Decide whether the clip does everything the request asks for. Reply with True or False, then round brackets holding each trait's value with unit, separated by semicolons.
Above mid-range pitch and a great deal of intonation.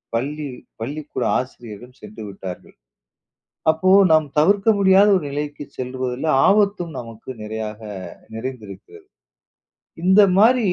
False (145 Hz; 8.6 semitones)